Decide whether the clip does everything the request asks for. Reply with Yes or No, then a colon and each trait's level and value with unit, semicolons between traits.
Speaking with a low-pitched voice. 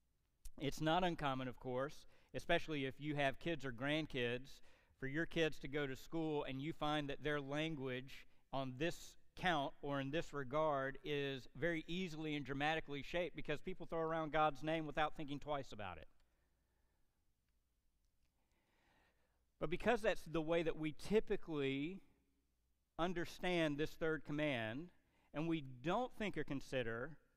No: medium, 150 Hz